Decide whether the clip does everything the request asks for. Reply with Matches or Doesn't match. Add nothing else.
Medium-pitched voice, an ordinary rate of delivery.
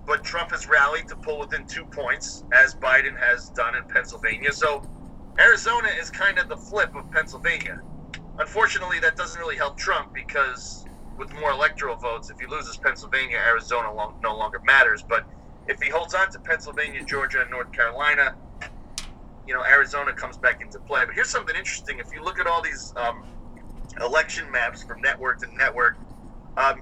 Matches